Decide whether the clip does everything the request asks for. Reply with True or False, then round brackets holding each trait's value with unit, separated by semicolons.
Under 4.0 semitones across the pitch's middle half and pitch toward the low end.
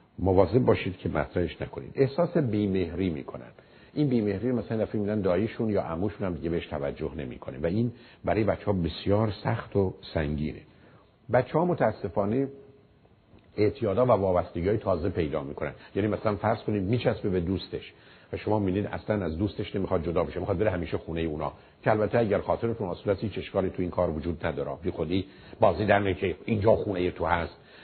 True (3.5 semitones; 100 Hz)